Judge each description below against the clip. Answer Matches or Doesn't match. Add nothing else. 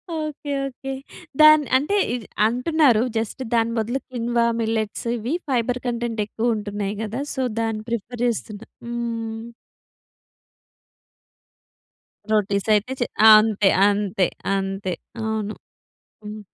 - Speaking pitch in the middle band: Doesn't match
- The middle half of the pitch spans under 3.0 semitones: Matches